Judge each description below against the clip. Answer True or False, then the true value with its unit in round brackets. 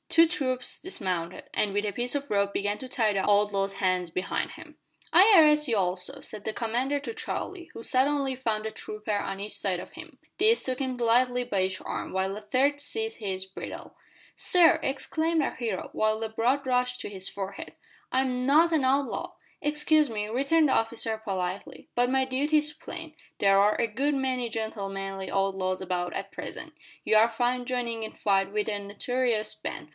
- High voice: True (230 Hz)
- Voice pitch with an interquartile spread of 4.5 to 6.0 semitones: True (5.2 semitones)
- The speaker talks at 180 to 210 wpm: True (190 wpm)